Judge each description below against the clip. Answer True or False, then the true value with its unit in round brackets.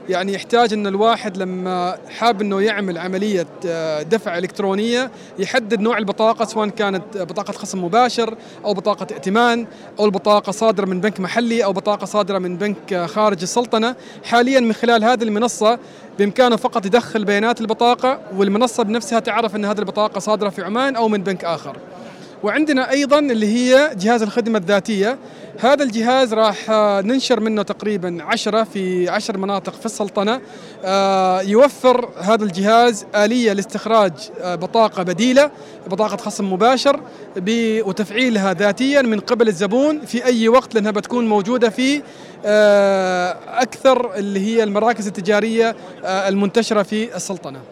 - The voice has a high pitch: True (215 Hz)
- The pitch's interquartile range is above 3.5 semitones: False (3.0 semitones)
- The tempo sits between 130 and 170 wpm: True (135 wpm)